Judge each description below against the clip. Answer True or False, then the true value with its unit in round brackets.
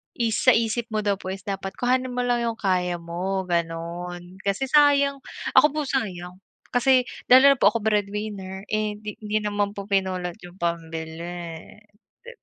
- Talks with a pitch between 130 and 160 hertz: False (200 Hz)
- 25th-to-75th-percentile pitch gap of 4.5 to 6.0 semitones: True (4.8 semitones)